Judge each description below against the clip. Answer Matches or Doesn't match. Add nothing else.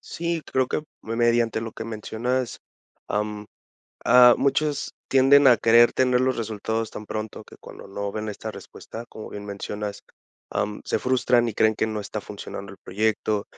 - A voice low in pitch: Matches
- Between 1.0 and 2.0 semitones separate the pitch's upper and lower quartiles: Doesn't match